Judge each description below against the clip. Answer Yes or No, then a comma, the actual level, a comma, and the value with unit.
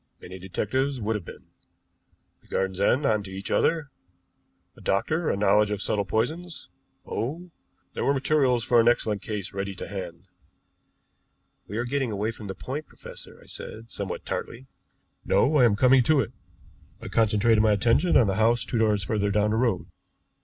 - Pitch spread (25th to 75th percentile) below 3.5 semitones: No, average, 4.3 semitones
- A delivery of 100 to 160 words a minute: No, average, 180 wpm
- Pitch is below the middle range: Yes, low, 110 Hz